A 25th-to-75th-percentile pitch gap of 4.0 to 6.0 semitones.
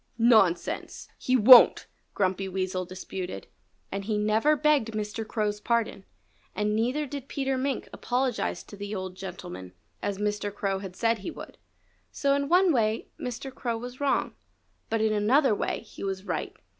Yes: average, 4.5 semitones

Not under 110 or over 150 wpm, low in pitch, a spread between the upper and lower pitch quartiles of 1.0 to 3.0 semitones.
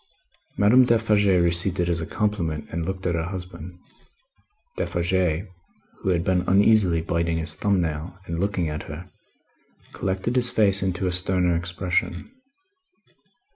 Yes: average, 140 wpm; very low, 90 Hz; narrow, 2.5 semitones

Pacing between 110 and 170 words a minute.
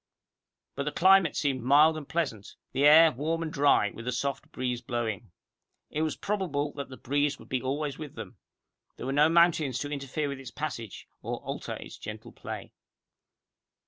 No: average, 180 wpm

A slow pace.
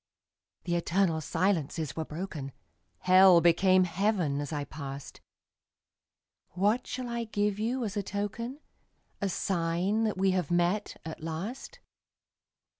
Yes: slow, 125 wpm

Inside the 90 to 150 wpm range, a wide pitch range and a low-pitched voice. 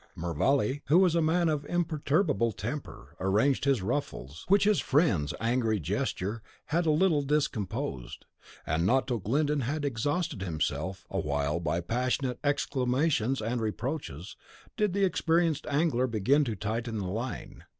Yes: average, 140 wpm; wide, 6.6 semitones; low, 130 Hz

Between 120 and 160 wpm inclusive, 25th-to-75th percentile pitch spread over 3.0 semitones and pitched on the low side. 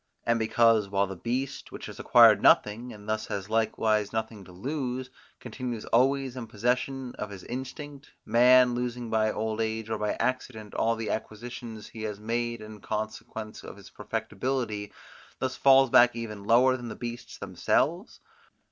No: average, 155 wpm; average, 2.7 semitones; low, 115 Hz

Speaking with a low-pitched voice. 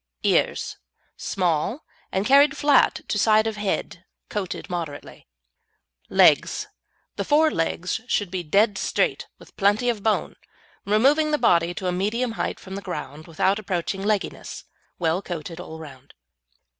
No: high, 195 Hz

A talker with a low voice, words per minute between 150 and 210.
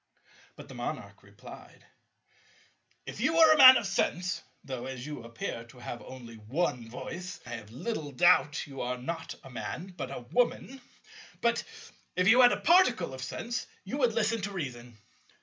No: medium, 165 Hz; average, 165 wpm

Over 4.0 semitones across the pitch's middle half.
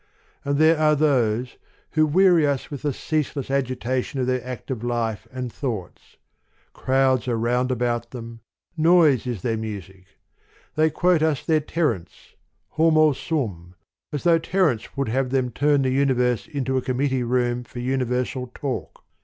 No: average, 3.5 semitones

